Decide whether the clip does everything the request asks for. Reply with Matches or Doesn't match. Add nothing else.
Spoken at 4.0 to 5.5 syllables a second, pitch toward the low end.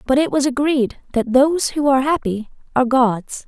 Doesn't match